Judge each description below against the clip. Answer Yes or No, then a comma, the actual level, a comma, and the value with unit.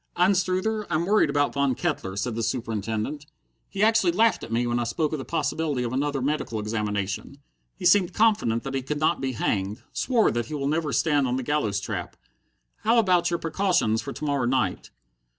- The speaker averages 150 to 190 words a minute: No, average, 200 wpm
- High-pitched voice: No, medium, 140 Hz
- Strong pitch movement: Yes, wide, 6.9 semitones